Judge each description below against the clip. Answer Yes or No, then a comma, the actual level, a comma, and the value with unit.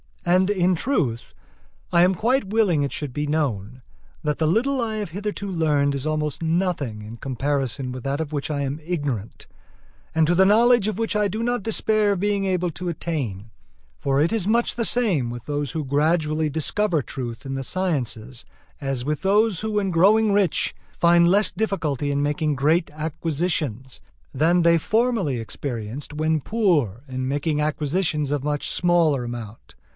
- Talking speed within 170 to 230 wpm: Yes, average, 175 wpm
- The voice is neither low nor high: Yes, medium, 155 Hz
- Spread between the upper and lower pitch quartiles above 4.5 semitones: Yes, wide, 5.6 semitones